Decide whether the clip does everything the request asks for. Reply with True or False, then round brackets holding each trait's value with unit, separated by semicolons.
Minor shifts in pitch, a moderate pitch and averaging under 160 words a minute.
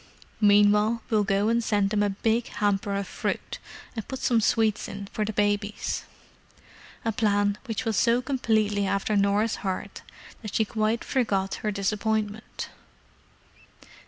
False (1.6 semitones; 210 Hz; 145 wpm)